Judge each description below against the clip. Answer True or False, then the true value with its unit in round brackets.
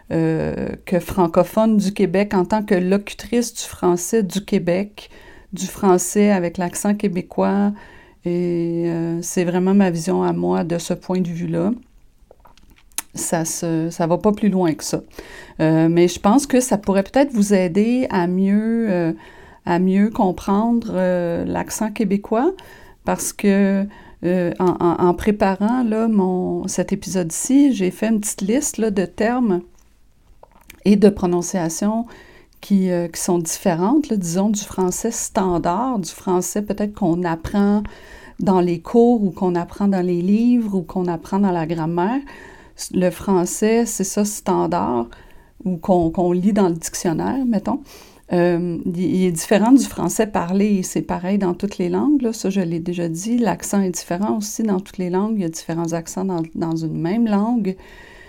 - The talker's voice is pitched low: False (190 Hz)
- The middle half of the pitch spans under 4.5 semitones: True (3.2 semitones)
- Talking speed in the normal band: True (165 wpm)